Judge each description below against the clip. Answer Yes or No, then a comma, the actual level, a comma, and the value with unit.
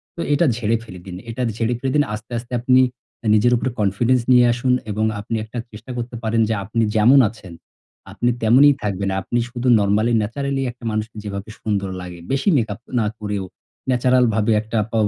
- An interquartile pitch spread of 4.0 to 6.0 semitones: No, average, 2.9 semitones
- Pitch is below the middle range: Yes, low, 115 Hz